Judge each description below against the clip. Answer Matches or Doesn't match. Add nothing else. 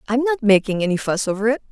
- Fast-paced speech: Matches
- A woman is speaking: Matches